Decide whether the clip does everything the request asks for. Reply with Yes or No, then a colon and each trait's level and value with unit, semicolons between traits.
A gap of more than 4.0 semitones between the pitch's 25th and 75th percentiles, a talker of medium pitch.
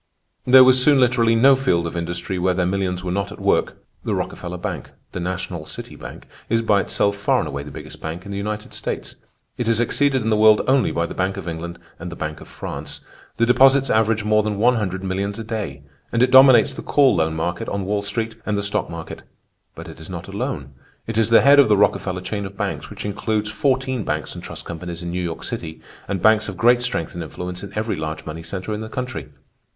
No: average, 4.4 semitones; low, 100 Hz